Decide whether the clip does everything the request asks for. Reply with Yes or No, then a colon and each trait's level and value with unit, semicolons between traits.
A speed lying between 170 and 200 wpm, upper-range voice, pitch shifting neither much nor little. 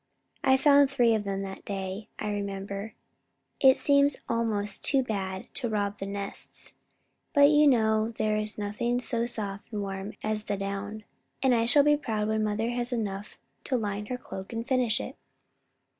Yes: average, 180 wpm; high, 215 Hz; average, 3.4 semitones